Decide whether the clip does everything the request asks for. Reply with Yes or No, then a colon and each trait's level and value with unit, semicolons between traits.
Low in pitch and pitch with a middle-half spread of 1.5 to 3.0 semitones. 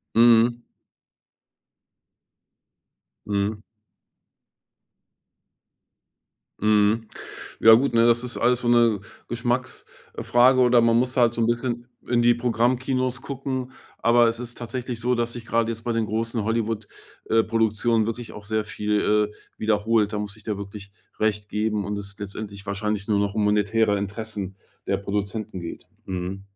Yes: low, 110 Hz; narrow, 2.4 semitones